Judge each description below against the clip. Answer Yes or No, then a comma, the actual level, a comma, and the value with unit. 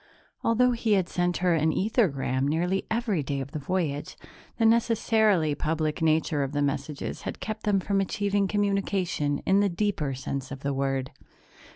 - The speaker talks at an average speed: Yes, average, 170 wpm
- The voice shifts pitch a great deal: Yes, wide, 6.1 semitones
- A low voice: No, medium, 175 Hz